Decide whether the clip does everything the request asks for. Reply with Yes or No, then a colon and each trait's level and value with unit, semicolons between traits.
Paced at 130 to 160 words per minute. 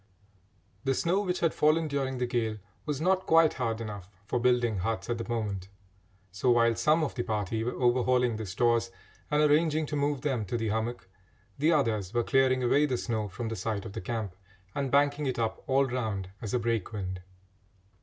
No: average, 200 wpm